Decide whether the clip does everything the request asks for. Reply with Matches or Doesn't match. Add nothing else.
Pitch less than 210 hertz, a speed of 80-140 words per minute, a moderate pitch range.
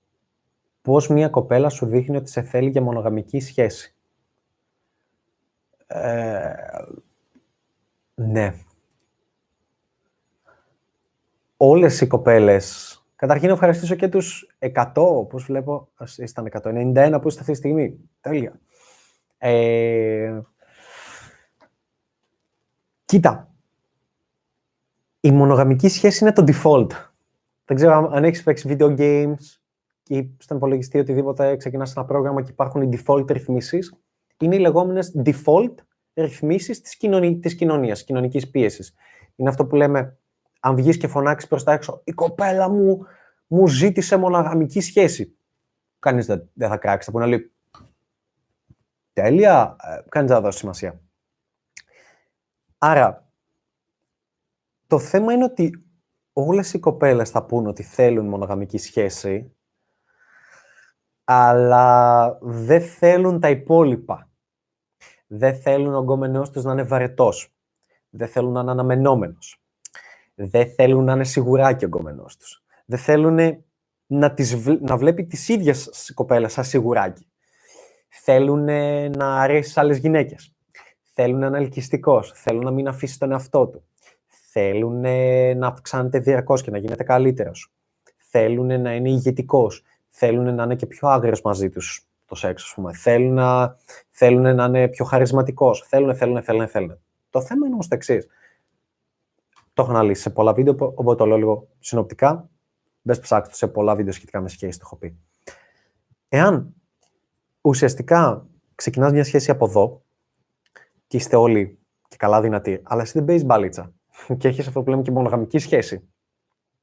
Matches